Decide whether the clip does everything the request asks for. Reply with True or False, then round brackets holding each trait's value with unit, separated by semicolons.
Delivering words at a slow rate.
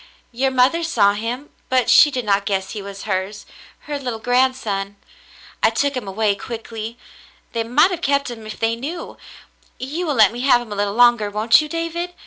False (200 wpm)